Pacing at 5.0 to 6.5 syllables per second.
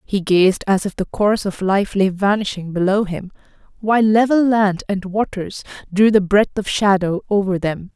No: 4.8 syllables/s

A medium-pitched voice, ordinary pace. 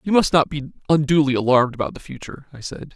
No: medium, 145 Hz; fast, 225 wpm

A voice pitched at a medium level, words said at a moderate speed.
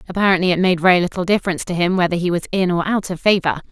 No: medium, 180 Hz; fast, 260 wpm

